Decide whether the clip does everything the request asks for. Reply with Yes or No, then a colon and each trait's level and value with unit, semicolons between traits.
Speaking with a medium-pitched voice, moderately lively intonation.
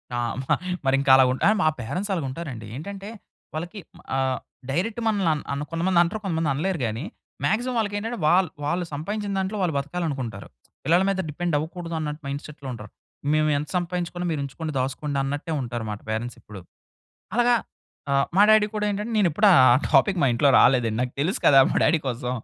No: medium, 160 Hz; wide, 5.8 semitones